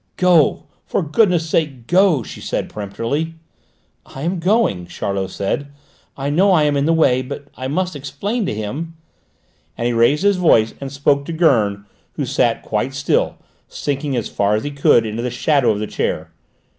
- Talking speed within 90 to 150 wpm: No, average, 180 wpm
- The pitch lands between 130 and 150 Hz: Yes, medium, 140 Hz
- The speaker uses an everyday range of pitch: No, wide, 6.0 semitones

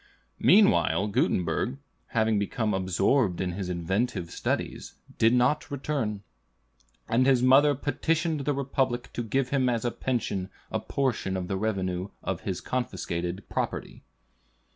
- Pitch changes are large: Yes, wide, 5.8 semitones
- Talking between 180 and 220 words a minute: No, slow, 135 wpm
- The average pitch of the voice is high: No, low, 115 Hz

